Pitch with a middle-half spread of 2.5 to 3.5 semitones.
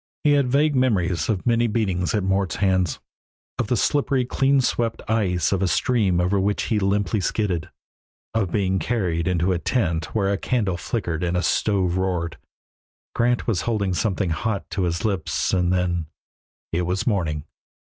No: average, 4.2 semitones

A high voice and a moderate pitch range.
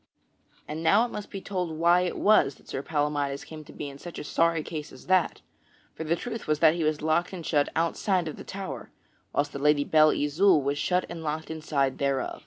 No: medium, 155 Hz; average, 3.1 semitones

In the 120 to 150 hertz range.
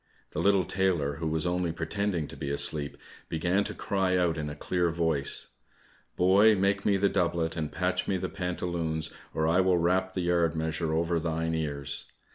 No: very low, 85 Hz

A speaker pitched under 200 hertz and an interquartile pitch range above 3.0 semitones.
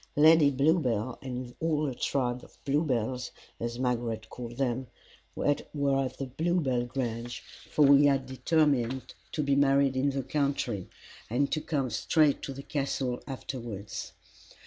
No: low, 135 Hz; average, 2.7 semitones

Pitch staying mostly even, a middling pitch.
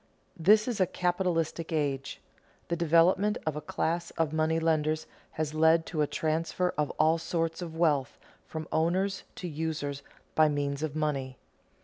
Yes: narrow, 2.0 semitones; medium, 160 Hz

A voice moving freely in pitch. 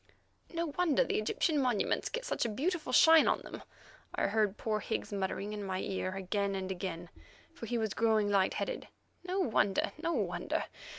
Yes: wide, 6.8 semitones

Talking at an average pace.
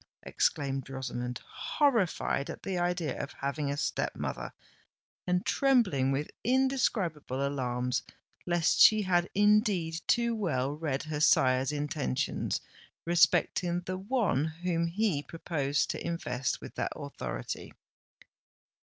No: slow, 120 wpm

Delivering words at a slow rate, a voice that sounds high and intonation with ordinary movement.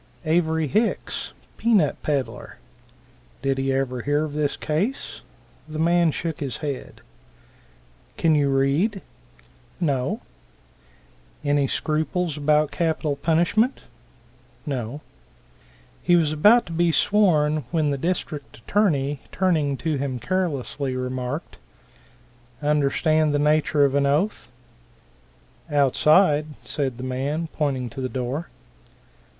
No: slow, 115 wpm; medium, 150 Hz; average, 3.1 semitones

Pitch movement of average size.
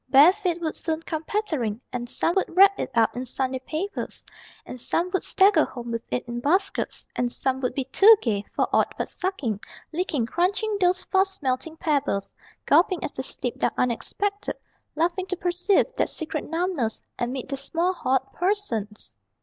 No: wide, 6.7 semitones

